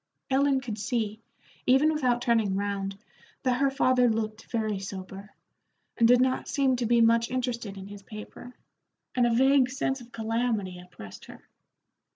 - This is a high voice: Yes, high, 235 Hz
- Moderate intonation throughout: Yes, average, 3.7 semitones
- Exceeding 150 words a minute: Yes, average, 160 wpm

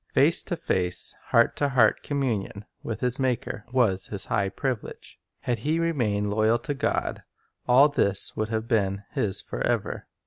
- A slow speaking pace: No, average, 160 wpm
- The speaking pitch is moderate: No, low, 115 Hz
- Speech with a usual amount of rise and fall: Yes, average, 4.3 semitones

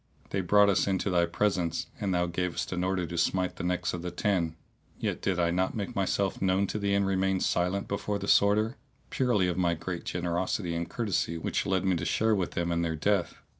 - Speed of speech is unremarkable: No, fast, 220 wpm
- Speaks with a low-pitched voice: Yes, very low, 95 Hz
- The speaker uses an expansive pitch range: No, narrow, 2.4 semitones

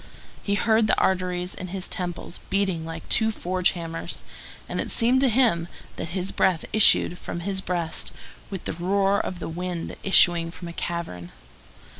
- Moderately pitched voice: Yes, medium, 180 Hz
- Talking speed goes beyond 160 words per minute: Yes, average, 170 wpm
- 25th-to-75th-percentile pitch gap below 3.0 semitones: Yes, narrow, 2.6 semitones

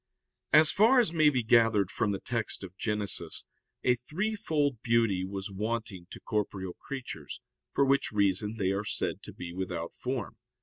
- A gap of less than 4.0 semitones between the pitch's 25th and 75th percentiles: No, wide, 5.6 semitones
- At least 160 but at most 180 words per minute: Yes, average, 165 wpm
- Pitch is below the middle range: Yes, low, 110 Hz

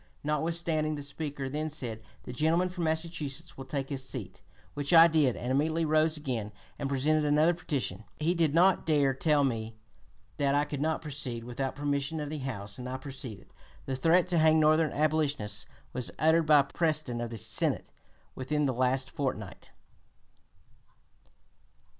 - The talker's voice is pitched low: No, medium, 145 Hz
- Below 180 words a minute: Yes, average, 170 wpm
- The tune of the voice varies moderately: Yes, average, 3.1 semitones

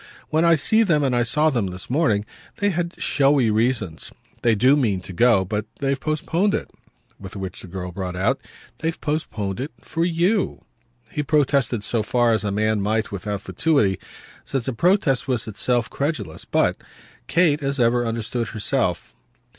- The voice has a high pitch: No, low, 120 Hz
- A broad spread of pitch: Yes, wide, 6.2 semitones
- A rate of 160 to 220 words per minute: Yes, average, 170 wpm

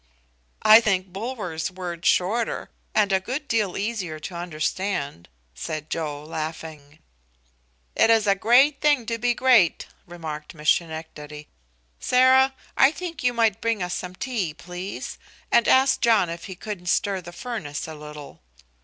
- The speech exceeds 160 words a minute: No, average, 150 wpm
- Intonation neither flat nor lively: No, wide, 6.4 semitones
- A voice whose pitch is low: No, medium, 185 Hz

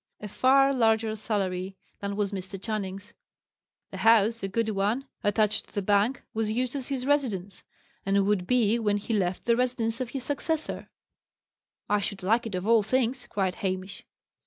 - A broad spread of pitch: No, average, 3.3 semitones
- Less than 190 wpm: Yes, average, 175 wpm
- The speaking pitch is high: Yes, high, 215 Hz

